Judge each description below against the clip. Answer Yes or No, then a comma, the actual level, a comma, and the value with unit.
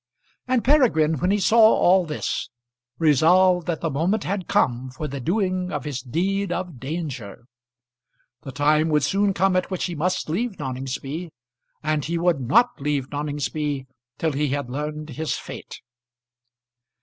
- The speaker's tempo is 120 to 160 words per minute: Yes, average, 155 wpm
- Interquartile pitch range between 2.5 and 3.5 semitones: No, average, 4.4 semitones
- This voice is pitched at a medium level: Yes, medium, 155 Hz